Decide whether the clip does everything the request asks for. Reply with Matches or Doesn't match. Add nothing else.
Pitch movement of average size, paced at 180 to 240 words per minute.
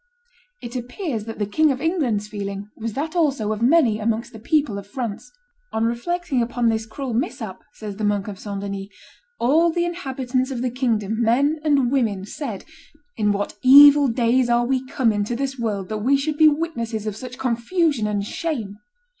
Matches